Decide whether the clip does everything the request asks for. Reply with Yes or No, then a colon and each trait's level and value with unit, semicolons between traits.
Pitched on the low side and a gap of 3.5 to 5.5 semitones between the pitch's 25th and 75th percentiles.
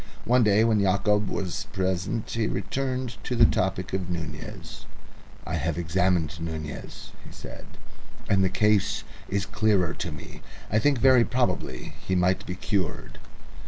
Yes: very low, 95 Hz; average, 3.8 semitones